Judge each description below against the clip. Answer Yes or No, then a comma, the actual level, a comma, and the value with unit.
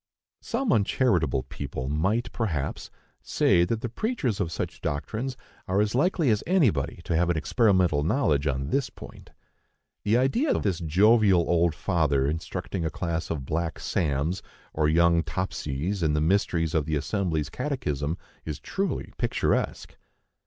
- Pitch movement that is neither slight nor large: No, wide, 6.0 semitones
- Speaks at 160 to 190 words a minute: No, average, 150 wpm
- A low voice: Yes, very low, 85 Hz